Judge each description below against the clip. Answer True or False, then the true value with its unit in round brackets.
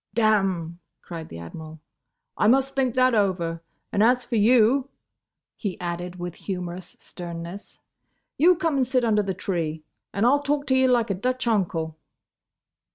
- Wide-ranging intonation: True (6.6 semitones)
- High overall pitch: True (205 Hz)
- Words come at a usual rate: True (160 wpm)